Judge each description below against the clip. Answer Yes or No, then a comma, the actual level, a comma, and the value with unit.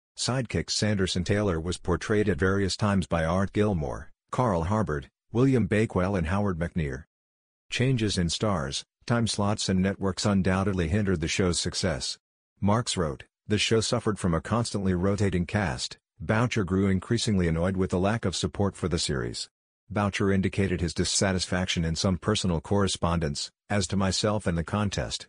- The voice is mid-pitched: No, very low, 95 Hz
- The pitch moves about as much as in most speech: Yes, average, 3.1 semitones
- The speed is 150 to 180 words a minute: Yes, average, 155 wpm